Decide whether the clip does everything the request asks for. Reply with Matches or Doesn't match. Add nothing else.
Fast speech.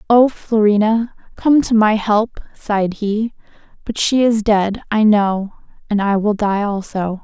Doesn't match